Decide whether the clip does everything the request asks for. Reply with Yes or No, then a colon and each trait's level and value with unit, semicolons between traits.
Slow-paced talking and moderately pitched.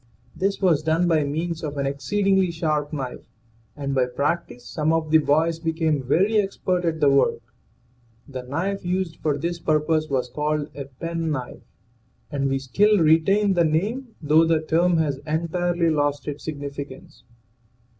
No: average, 160 wpm; medium, 160 Hz